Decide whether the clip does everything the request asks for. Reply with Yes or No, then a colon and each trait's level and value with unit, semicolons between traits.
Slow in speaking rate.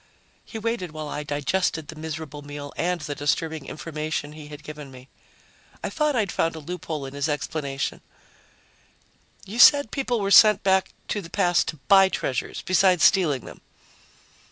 No: average, 165 wpm